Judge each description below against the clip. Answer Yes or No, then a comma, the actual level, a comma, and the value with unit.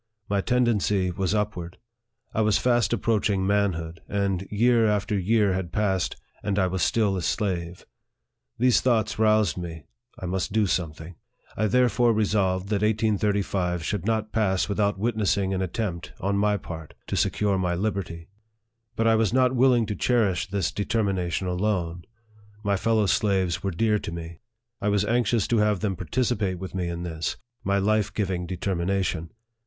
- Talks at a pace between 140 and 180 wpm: Yes, average, 165 wpm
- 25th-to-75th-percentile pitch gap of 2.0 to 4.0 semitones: Yes, average, 2.9 semitones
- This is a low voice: Yes, low, 100 Hz